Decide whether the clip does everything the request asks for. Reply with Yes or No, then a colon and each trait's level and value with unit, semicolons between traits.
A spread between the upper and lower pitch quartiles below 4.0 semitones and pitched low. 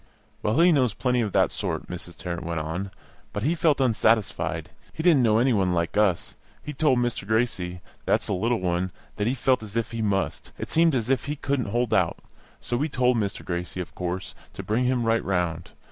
No: wide, 5.6 semitones; low, 110 Hz